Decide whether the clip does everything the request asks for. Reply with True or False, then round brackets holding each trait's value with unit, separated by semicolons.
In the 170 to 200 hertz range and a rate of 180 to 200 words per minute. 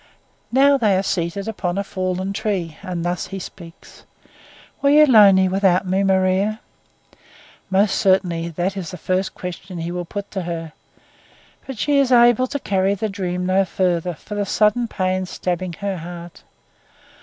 False (190 Hz; 165 wpm)